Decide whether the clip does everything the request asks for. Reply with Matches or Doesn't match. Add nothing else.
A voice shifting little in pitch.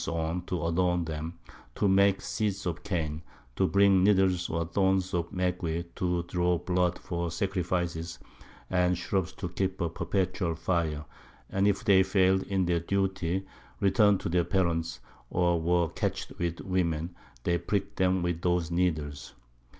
Matches